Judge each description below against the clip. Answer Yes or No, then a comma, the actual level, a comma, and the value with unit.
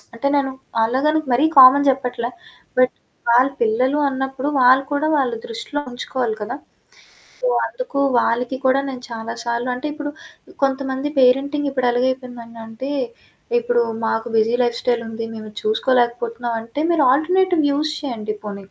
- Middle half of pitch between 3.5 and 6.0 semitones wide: No, average, 3.0 semitones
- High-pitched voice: Yes, very high, 255 Hz